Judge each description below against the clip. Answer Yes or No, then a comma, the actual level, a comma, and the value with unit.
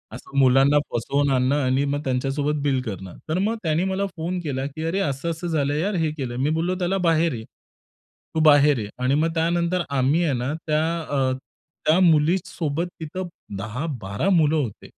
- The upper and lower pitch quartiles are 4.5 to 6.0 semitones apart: No, average, 3.7 semitones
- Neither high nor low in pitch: Yes, medium, 150 Hz